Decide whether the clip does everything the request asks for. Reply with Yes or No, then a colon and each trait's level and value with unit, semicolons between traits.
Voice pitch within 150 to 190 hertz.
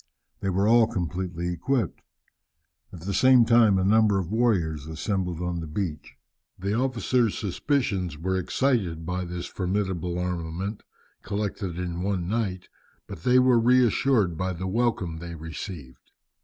No: very low, 95 Hz